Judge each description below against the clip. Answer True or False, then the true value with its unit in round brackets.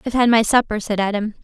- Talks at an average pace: False (250 wpm)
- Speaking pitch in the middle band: False (220 Hz)